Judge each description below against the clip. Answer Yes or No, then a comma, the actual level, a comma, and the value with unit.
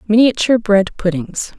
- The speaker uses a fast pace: No, slow, 115 wpm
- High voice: Yes, high, 210 Hz